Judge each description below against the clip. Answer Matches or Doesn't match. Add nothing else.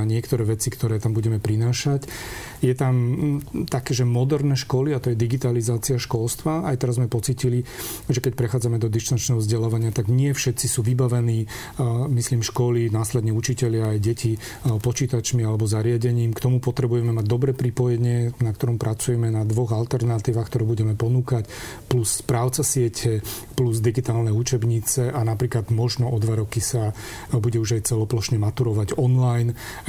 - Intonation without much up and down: Matches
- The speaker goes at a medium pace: Matches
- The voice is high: Doesn't match